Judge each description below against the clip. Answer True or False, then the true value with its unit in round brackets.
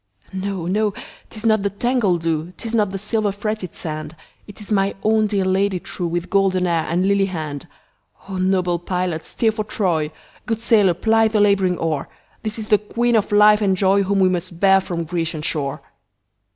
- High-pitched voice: True (195 Hz)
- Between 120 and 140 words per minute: False (165 wpm)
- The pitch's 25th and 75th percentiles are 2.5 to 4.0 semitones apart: True (3.3 semitones)